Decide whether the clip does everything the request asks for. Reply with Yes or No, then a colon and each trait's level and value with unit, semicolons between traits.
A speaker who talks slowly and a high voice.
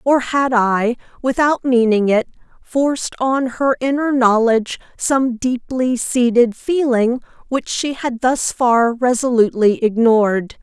Yes: slow, 125 wpm; high, 245 Hz